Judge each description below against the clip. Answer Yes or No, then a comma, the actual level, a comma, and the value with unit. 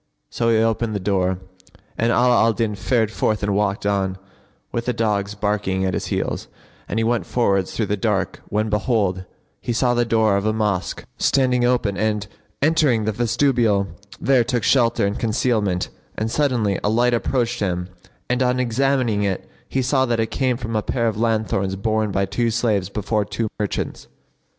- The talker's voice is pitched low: Yes, low, 110 Hz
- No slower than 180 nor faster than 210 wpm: Yes, average, 185 wpm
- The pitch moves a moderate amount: Yes, average, 3.0 semitones